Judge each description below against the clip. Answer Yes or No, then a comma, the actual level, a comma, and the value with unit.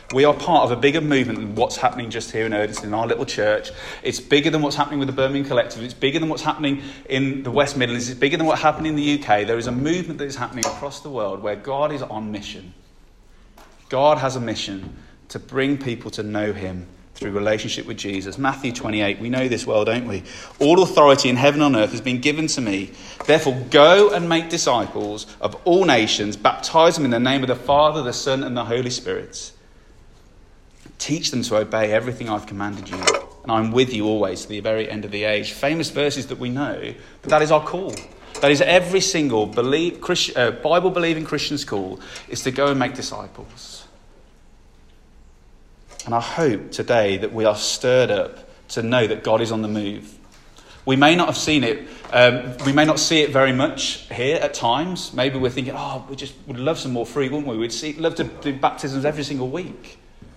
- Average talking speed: No, fast, 215 wpm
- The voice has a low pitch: Yes, low, 130 Hz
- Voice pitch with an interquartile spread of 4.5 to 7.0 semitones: Yes, average, 5.1 semitones